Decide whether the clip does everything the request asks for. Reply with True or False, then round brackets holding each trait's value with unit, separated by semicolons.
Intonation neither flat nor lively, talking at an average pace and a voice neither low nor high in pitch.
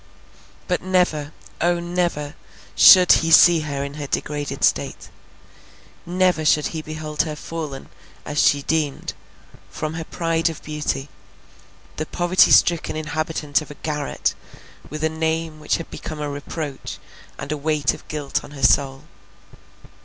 False (1.9 semitones; 145 wpm; 155 Hz)